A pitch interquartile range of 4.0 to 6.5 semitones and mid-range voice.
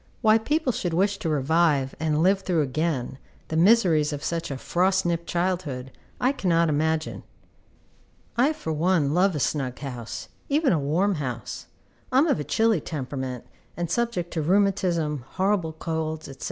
Yes: average, 4.4 semitones; medium, 165 Hz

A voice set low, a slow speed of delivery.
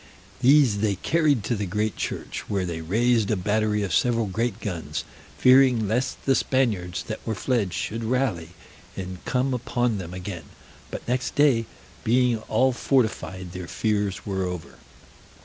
No: low, 110 Hz; average, 155 wpm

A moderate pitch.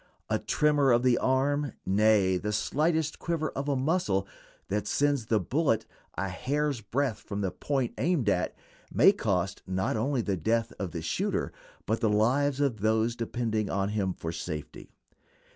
No: low, 115 Hz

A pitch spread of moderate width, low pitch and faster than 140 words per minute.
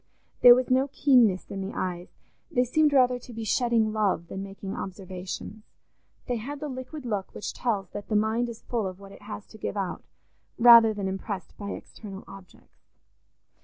No: average, 3.9 semitones; high, 215 Hz; average, 185 wpm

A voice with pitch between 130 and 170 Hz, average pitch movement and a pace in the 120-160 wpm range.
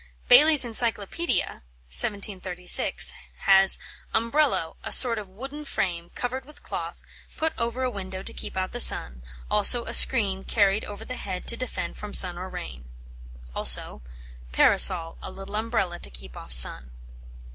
No: high, 200 Hz; average, 5.0 semitones; average, 150 wpm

